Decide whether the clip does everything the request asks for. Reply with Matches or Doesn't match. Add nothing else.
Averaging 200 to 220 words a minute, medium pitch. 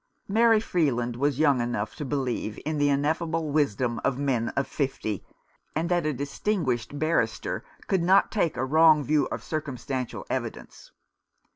Doesn't match